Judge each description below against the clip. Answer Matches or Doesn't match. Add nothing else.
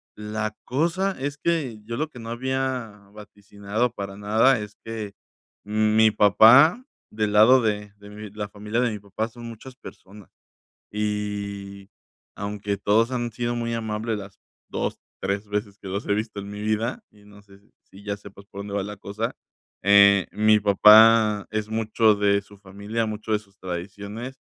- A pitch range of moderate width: Doesn't match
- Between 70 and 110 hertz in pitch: Matches